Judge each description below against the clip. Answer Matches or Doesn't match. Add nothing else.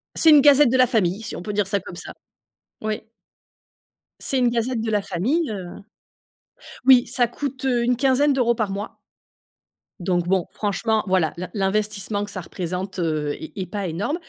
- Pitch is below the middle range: Doesn't match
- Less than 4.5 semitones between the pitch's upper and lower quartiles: Doesn't match